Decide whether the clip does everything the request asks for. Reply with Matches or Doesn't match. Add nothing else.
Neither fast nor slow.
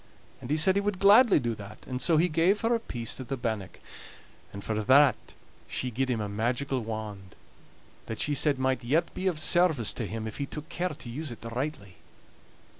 Doesn't match